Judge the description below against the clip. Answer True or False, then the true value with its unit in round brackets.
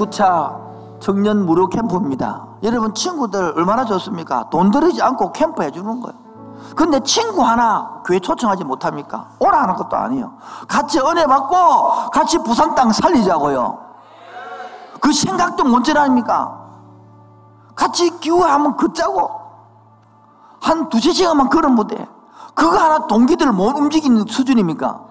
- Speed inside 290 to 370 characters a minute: True (300 characters per minute)